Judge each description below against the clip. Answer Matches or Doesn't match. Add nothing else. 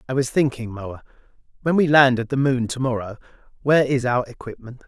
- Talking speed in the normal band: Matches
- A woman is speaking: Doesn't match